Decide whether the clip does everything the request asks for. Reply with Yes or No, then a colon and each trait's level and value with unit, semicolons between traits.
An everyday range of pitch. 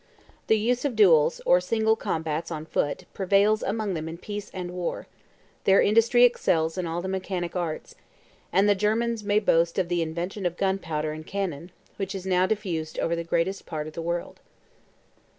Yes: average, 3.6 semitones